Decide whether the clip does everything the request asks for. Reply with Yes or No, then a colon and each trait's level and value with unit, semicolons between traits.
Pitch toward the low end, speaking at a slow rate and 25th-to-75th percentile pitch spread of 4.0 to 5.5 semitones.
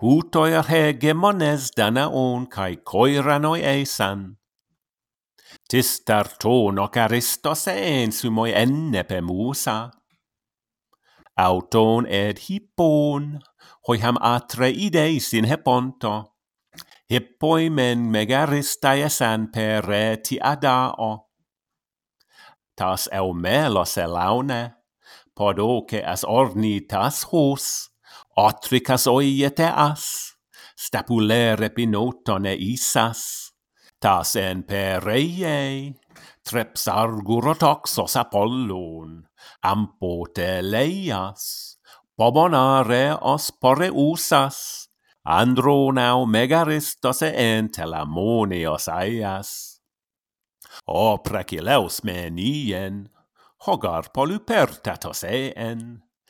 Yes: low, 120 Hz; slow, 80 wpm; average, 4.7 semitones